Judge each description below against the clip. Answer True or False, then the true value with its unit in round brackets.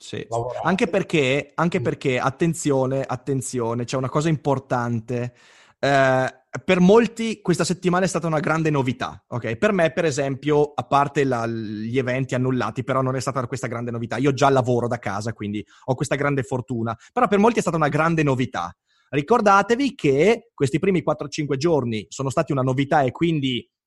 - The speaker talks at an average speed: False (175 wpm)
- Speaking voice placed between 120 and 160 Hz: True (140 Hz)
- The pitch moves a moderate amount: True (4.2 semitones)